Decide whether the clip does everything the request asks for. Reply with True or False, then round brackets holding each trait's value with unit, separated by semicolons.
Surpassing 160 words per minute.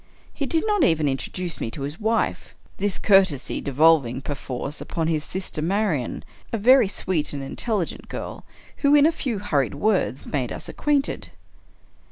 True (170 wpm)